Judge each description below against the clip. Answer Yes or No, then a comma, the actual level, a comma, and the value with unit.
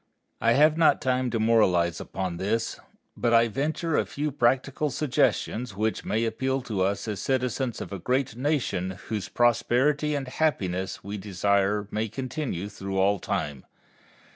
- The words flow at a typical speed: Yes, average, 155 wpm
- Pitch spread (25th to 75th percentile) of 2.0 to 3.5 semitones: No, average, 5.0 semitones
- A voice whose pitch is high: No, low, 115 Hz